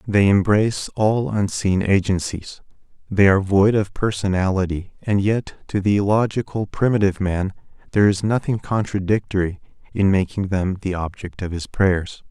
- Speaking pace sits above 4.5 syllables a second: Yes, 5.0 syllables/s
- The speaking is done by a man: Yes, male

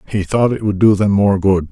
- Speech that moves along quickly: Yes, fast, 280 wpm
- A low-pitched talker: Yes, low, 100 Hz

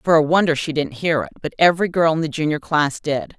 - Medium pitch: Yes, medium, 155 Hz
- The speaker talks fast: Yes, fast, 265 wpm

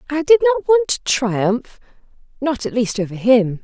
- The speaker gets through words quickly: No, average, 165 wpm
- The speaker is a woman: Yes, female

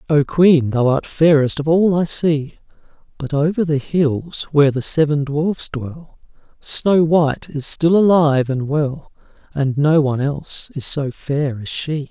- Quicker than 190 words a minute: No, average, 170 wpm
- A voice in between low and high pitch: Yes, medium, 150 Hz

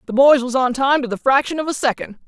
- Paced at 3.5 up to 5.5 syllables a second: No, 6.3 syllables/s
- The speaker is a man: No, female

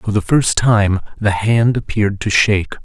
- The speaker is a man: Yes, male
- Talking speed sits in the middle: Yes, average, 190 wpm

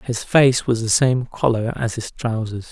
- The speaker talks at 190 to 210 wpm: Yes, average, 200 wpm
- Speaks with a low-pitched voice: Yes, low, 120 Hz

